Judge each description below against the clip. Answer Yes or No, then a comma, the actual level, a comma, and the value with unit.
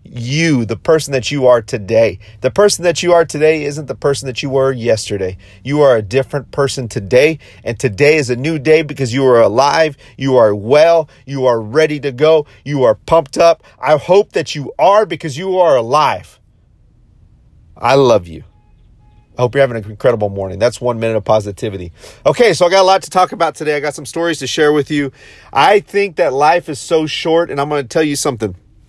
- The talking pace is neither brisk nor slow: No, fast, 215 wpm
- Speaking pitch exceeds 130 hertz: Yes, medium, 140 Hz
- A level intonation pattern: No, average, 4.8 semitones